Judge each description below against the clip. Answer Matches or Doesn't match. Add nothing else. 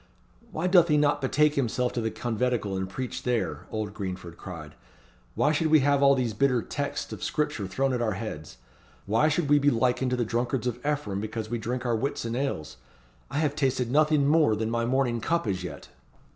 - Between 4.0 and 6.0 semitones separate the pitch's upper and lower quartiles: Matches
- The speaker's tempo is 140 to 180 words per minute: Doesn't match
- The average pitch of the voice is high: Doesn't match